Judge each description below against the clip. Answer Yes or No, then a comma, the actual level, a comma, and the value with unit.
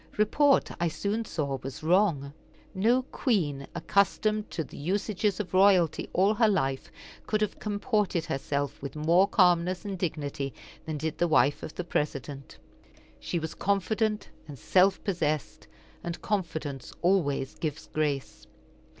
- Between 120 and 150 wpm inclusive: Yes, average, 140 wpm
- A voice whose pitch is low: No, medium, 175 Hz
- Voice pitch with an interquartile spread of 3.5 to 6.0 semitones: Yes, wide, 5.5 semitones